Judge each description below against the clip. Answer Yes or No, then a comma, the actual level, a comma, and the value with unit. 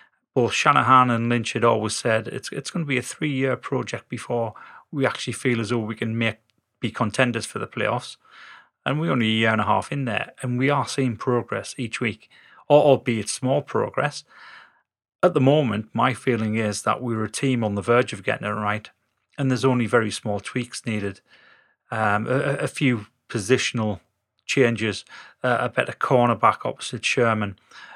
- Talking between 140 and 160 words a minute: No, average, 180 wpm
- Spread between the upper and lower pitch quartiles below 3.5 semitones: Yes, average, 2.9 semitones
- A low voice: Yes, low, 120 Hz